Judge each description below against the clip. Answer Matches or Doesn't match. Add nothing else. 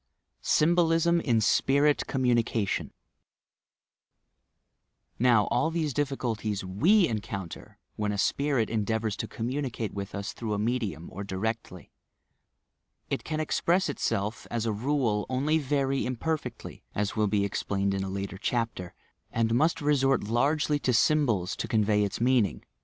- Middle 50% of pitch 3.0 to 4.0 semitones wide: Doesn't match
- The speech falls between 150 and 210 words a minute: Doesn't match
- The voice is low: Matches